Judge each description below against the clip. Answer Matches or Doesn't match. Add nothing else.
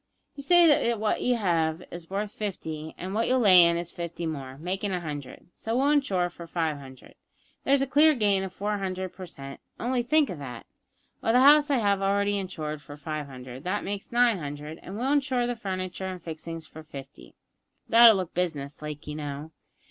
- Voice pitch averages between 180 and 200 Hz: Matches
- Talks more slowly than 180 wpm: Doesn't match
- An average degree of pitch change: Doesn't match